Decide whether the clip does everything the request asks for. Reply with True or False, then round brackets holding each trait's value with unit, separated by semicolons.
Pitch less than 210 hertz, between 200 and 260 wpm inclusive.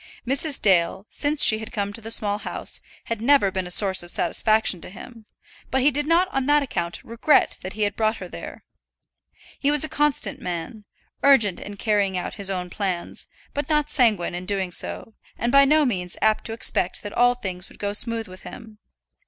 False (215 Hz; 205 wpm)